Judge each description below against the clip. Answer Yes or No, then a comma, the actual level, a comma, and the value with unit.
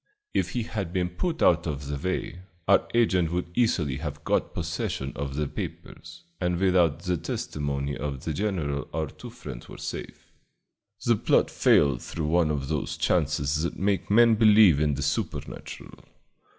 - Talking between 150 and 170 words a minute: Yes, average, 165 wpm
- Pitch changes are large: No, average, 4.4 semitones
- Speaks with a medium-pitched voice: No, very low, 80 Hz